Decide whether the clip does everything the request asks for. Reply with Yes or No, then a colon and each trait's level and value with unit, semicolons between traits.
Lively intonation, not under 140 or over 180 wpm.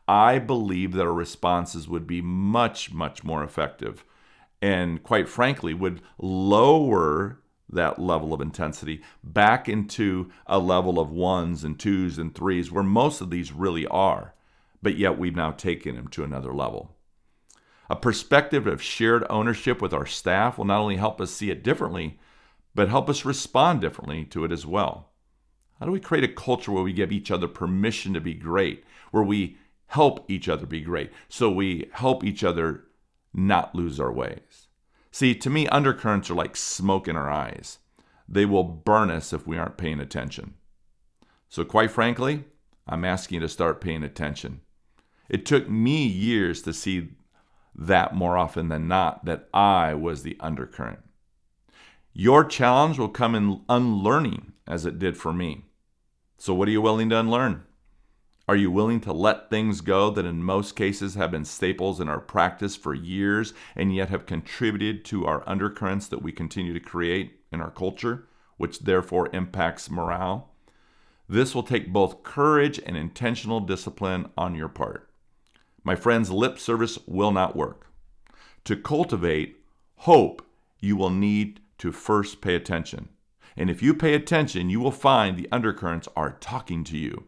No: average, 4.3 semitones; average, 170 wpm